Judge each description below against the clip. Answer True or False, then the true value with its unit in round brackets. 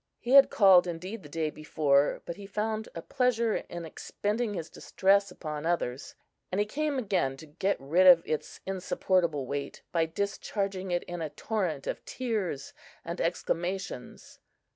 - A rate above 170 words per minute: False (160 wpm)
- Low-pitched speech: False (180 Hz)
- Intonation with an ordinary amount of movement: True (4.5 semitones)